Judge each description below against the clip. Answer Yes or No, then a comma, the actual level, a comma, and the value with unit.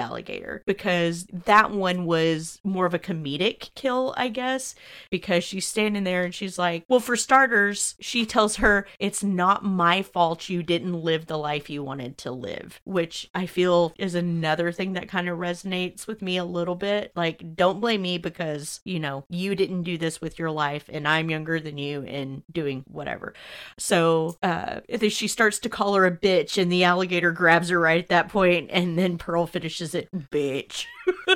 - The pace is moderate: Yes, average, 190 wpm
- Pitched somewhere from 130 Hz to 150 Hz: No, medium, 180 Hz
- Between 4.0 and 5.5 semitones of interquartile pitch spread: No, average, 3.1 semitones